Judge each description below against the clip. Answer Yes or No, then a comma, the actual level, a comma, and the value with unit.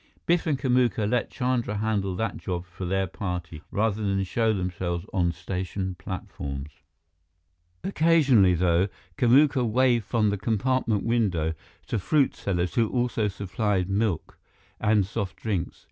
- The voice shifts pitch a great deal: No, average, 4.4 semitones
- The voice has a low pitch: Yes, low, 105 Hz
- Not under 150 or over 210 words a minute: No, slow, 135 wpm